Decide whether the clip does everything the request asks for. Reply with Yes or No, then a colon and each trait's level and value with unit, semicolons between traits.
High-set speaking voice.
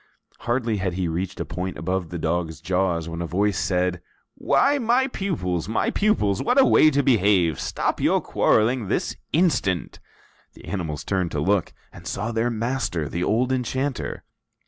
No: very low, 95 Hz